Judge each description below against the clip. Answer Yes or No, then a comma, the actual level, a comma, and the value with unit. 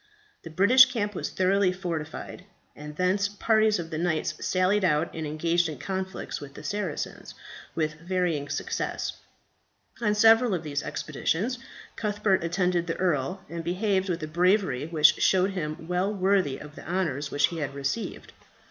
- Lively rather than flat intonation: No, average, 3.9 semitones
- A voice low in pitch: No, medium, 180 Hz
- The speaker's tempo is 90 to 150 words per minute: No, average, 160 wpm